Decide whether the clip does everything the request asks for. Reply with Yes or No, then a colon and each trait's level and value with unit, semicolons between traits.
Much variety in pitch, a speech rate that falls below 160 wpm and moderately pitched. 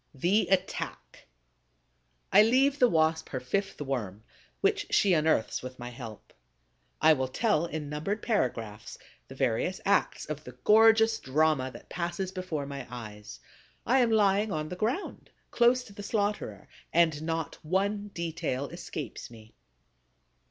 Yes: wide, 7.6 semitones; average, 145 wpm; medium, 165 Hz